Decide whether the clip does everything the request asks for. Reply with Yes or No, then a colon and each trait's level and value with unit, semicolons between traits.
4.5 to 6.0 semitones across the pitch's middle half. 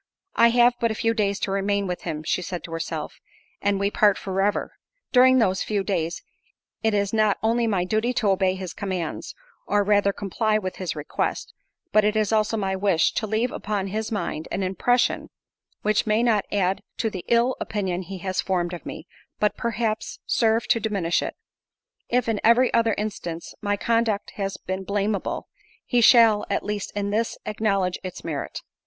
No: average, 2.7 semitones